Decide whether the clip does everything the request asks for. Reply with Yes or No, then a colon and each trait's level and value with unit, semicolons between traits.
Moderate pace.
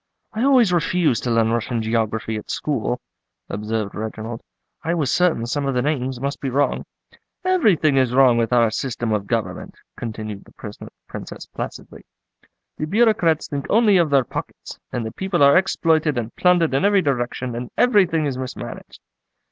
Yes: average, 165 wpm